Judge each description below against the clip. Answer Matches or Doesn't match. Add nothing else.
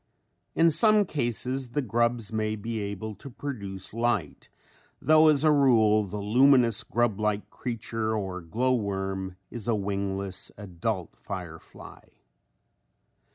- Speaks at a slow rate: Matches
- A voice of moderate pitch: Doesn't match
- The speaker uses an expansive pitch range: Doesn't match